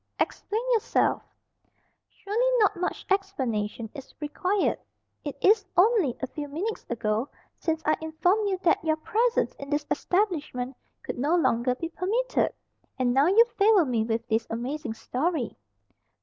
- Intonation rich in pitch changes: Yes, wide, 7.8 semitones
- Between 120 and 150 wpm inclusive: Yes, average, 145 wpm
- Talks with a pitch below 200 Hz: No, very high, 315 Hz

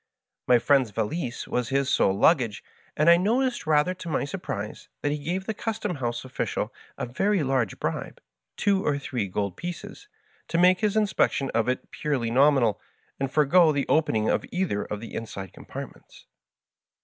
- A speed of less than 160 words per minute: No, average, 175 wpm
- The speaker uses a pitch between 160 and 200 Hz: No, medium, 140 Hz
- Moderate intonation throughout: No, wide, 7.2 semitones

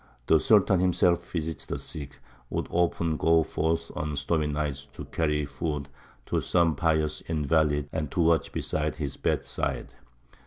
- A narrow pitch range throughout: Yes, narrow, 1.9 semitones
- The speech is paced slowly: No, average, 155 wpm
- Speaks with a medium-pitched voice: No, very low, 80 Hz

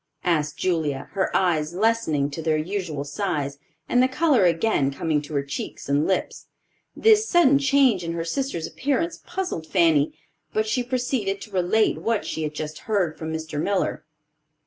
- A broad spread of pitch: Yes, wide, 6.9 semitones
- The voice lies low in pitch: No, medium, 175 Hz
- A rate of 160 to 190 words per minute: Yes, average, 170 wpm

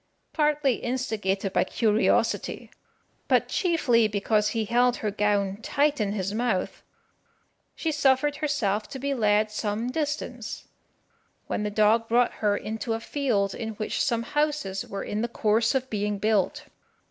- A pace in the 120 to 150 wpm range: Yes, average, 145 wpm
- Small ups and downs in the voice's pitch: No, average, 4.1 semitones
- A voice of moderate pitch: No, high, 225 Hz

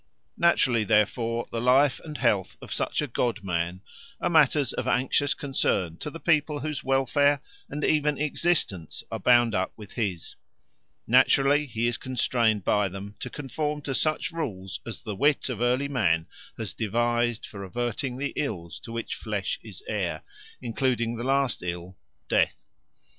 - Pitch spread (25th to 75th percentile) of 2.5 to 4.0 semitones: No, average, 5.2 semitones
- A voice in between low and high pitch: No, low, 120 Hz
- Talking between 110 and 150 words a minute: No, average, 160 wpm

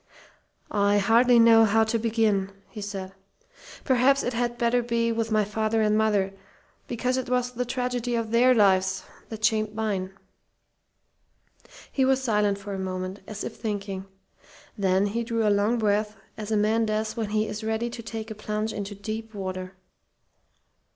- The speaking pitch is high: Yes, high, 220 Hz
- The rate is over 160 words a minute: Yes, average, 170 wpm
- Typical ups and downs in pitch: No, narrow, 2.3 semitones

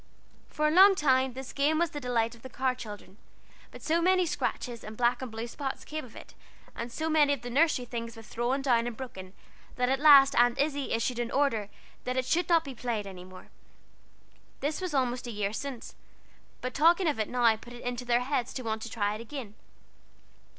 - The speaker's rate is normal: No, fast, 220 wpm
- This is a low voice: No, very high, 250 Hz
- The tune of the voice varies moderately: Yes, average, 3.7 semitones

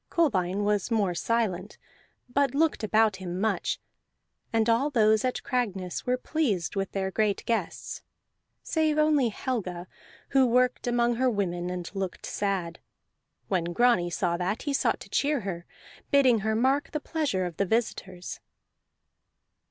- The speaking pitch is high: Yes, high, 220 Hz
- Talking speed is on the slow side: No, average, 145 wpm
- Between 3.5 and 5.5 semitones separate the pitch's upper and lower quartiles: Yes, average, 5.2 semitones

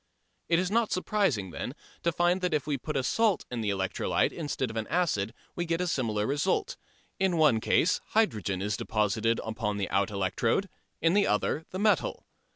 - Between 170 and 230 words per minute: Yes, average, 195 wpm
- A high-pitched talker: No, medium, 145 Hz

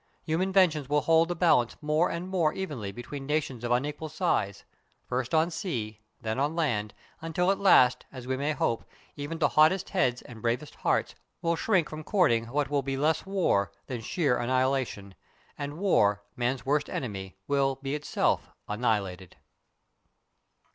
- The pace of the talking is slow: No, average, 160 wpm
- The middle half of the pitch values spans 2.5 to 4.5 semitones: No, average, 5.0 semitones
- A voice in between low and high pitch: Yes, medium, 145 Hz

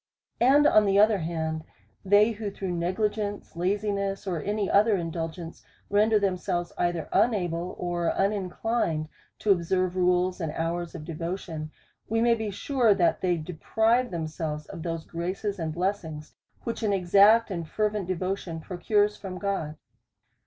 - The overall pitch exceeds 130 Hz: Yes, medium, 185 Hz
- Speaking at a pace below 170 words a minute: Yes, average, 150 wpm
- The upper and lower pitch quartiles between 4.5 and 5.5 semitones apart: No, average, 3.5 semitones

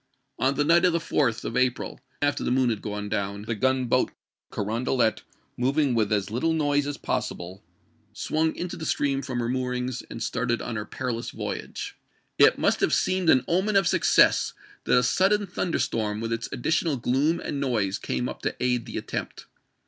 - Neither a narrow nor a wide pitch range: Yes, average, 4.2 semitones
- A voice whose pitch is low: Yes, low, 125 Hz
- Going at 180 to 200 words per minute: Yes, average, 185 wpm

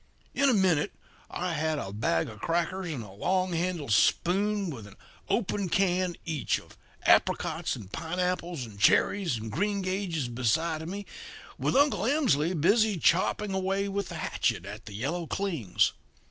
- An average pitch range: No, wide, 6.1 semitones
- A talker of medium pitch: Yes, medium, 175 Hz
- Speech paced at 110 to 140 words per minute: No, average, 160 wpm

